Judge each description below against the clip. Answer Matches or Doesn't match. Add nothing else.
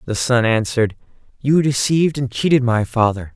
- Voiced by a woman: Doesn't match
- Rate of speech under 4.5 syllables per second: Doesn't match